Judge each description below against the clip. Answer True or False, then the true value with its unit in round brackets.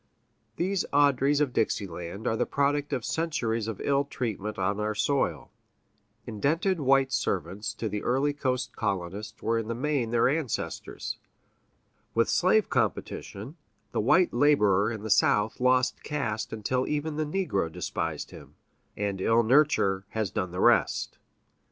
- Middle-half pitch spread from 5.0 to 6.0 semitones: True (5.4 semitones)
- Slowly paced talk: False (150 wpm)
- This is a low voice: True (120 Hz)